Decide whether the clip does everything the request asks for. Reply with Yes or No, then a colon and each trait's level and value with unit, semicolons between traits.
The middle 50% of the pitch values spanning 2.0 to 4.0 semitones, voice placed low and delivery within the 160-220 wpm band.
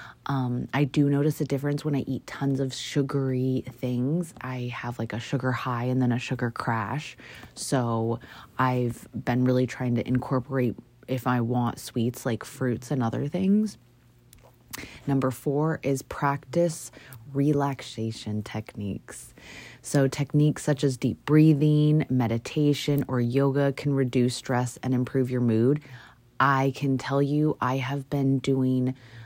No: narrow, 2.4 semitones; low, 130 Hz; average, 145 wpm